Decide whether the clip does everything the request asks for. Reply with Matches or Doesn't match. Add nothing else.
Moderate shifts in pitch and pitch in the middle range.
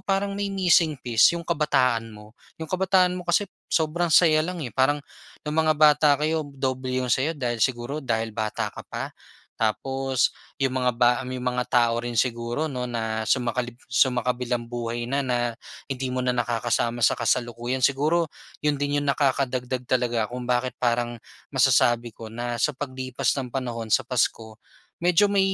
Doesn't match